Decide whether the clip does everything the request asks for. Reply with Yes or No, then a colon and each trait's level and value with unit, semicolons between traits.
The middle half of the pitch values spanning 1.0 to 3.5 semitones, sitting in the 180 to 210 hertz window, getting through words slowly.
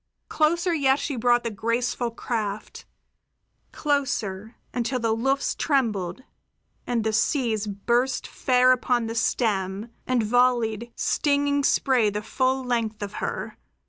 No: average, 3.1 semitones; high, 240 Hz; slow, 125 wpm